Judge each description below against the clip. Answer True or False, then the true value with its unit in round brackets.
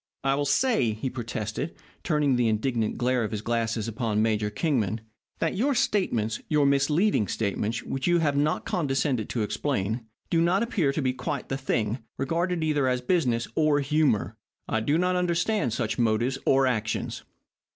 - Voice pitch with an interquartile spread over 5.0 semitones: True (5.5 semitones)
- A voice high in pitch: False (130 Hz)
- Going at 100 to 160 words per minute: False (170 wpm)